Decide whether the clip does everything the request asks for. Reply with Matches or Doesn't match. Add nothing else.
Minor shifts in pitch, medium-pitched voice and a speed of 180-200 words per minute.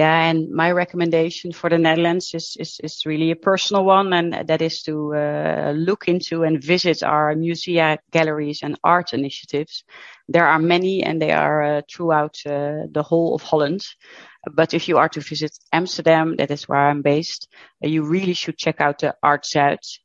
Matches